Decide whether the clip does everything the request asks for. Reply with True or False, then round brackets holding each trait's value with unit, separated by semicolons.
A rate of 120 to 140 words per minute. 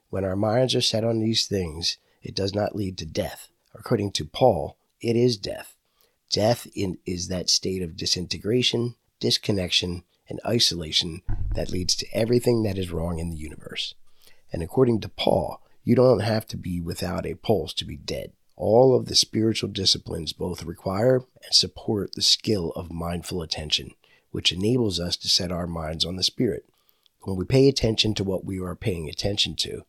False (180 wpm)